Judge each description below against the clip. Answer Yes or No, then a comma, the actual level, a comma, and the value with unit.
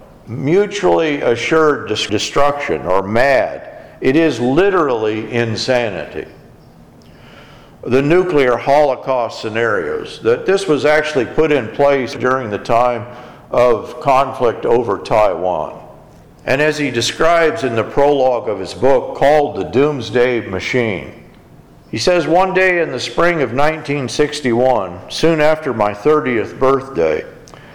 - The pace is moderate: No, slow, 120 wpm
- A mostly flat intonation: No, average, 4.7 semitones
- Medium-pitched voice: Yes, medium, 145 Hz